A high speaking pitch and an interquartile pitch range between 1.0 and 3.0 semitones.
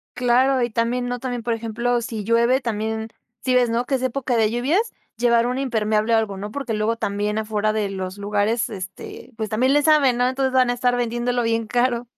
Yes: high, 235 Hz; narrow, 2.4 semitones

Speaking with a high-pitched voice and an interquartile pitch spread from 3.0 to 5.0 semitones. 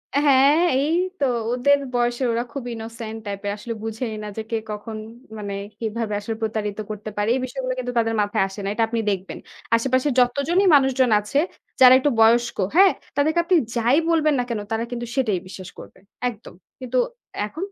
Yes: high, 235 Hz; average, 3.6 semitones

